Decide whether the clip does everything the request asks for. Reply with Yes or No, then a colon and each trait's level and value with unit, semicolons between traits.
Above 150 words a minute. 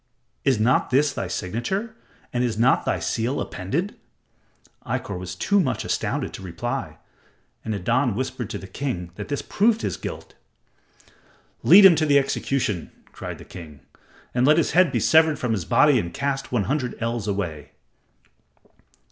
Yes: average, 165 wpm